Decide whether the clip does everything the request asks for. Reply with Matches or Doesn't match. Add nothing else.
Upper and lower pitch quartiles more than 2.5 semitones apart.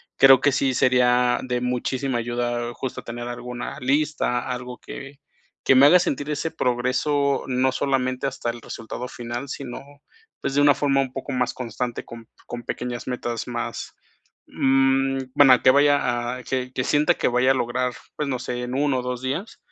Doesn't match